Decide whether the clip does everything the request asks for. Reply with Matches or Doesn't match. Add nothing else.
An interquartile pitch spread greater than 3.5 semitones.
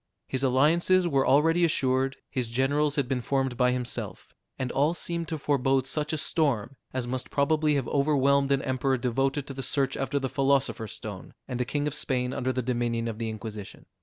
Doesn't match